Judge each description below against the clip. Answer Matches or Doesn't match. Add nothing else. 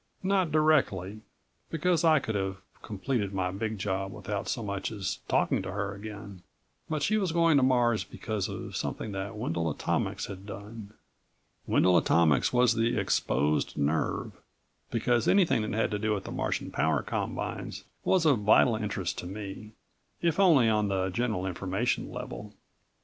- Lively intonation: Doesn't match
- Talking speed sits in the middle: Matches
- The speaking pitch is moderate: Doesn't match